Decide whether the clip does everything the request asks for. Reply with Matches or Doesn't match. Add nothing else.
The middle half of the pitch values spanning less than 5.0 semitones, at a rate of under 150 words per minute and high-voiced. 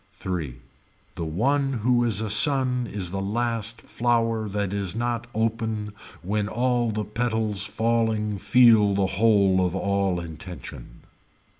Doesn't match